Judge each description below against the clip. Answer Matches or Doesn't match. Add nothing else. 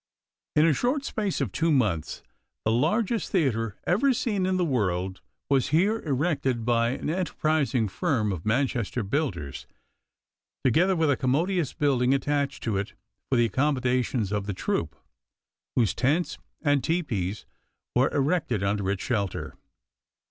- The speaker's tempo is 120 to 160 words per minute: Matches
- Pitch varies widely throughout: Matches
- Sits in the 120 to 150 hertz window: Matches